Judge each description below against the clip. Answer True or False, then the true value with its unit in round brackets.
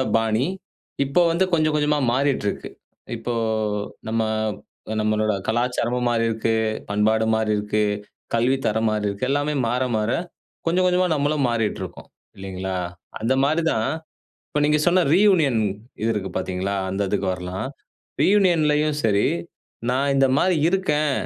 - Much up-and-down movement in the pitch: True (5.8 semitones)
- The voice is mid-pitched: False (120 Hz)